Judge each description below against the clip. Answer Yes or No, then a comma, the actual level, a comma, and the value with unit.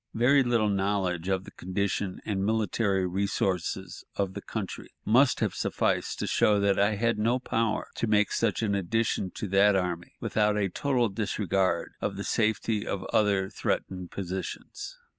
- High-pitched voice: No, low, 100 Hz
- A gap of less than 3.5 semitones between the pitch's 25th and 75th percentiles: Yes, narrow, 2.5 semitones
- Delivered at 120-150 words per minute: No, average, 160 wpm